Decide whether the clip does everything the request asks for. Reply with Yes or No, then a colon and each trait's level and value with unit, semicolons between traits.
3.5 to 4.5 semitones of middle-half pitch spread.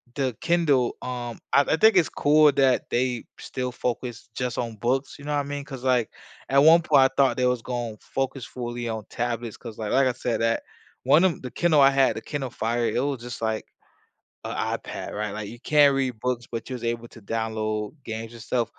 No: average, 2.9 semitones